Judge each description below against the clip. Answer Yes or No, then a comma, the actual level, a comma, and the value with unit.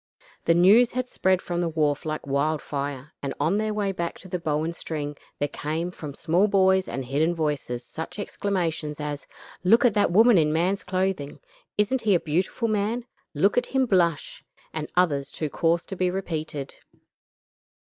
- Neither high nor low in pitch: Yes, medium, 170 Hz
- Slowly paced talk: No, average, 175 wpm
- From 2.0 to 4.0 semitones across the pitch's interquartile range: No, average, 4.5 semitones